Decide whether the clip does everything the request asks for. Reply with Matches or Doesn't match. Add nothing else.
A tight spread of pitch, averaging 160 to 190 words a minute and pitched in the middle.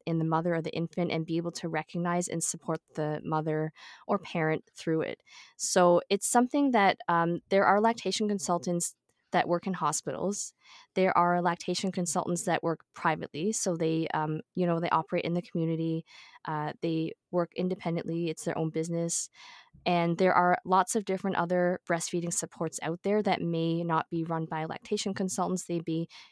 Matches